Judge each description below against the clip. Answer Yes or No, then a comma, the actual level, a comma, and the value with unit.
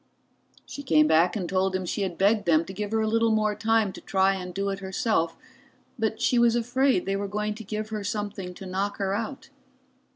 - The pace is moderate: No, fast, 225 wpm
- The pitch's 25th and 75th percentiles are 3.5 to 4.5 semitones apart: No, narrow, 2.6 semitones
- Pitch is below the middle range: No, high, 205 Hz